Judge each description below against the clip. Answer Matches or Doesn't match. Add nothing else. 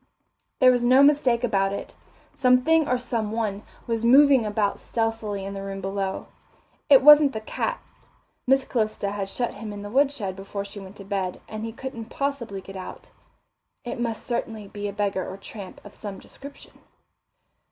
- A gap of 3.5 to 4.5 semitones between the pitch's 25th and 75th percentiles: Matches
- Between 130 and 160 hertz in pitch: Doesn't match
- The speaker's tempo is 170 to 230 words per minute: Matches